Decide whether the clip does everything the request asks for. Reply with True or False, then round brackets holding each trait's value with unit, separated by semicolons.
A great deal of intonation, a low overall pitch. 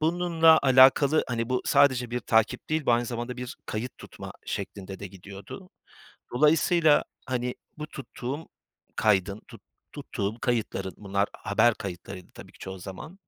True (6.3 semitones; 120 Hz)